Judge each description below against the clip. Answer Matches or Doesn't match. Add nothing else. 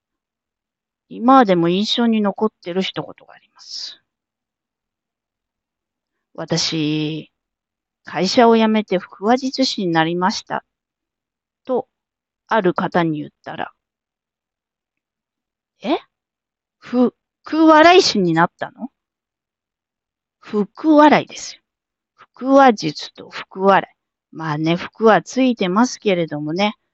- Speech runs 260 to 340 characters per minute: Doesn't match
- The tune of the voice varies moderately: Doesn't match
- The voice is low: Doesn't match